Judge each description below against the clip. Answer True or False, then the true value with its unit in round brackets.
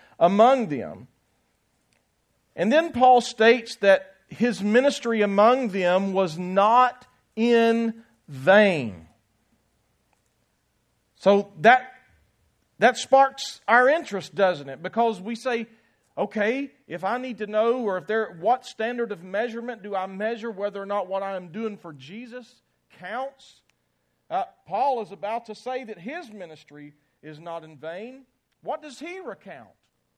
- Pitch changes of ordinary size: True (4.5 semitones)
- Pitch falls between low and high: False (220 Hz)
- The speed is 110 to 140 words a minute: True (135 wpm)